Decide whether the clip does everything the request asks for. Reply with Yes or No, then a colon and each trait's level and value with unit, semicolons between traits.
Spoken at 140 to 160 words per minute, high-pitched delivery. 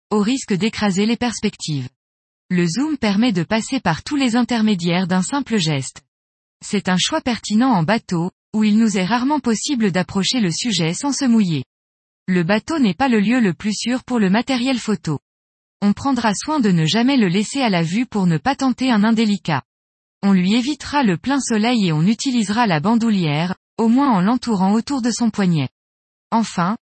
No: average, 190 wpm; high, 210 Hz